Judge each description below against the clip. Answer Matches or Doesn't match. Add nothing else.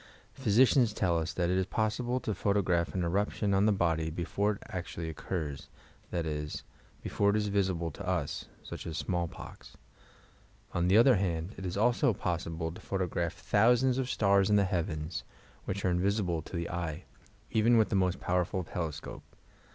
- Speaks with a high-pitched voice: Doesn't match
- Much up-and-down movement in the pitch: Doesn't match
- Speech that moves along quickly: Doesn't match